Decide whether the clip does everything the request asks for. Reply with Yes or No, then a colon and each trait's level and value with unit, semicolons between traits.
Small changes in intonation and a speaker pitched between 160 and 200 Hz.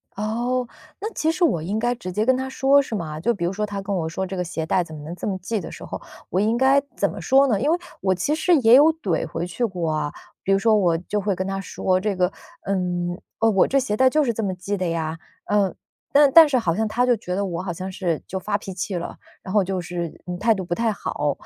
No: average, 5.1 semitones; high, 195 Hz